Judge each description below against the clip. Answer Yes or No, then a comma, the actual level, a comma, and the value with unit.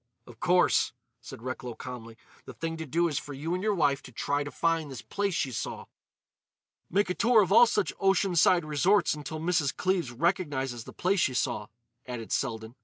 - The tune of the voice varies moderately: No, wide, 5.9 semitones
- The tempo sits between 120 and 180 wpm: No, average, 195 wpm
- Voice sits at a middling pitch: Yes, medium, 155 Hz